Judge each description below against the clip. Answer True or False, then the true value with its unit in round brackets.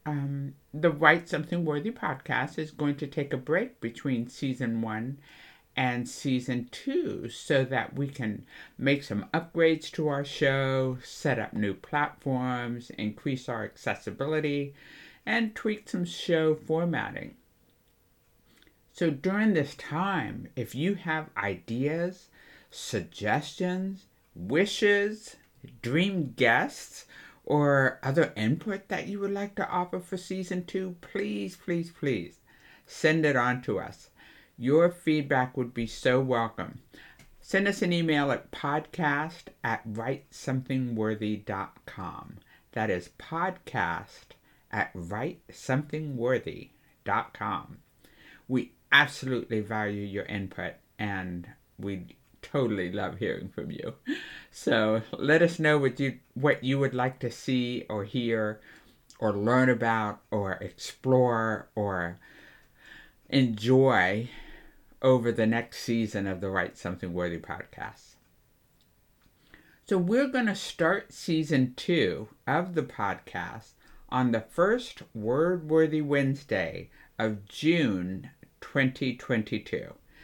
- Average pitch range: False (5.8 semitones)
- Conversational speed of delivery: False (115 wpm)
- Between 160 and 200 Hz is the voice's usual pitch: False (135 Hz)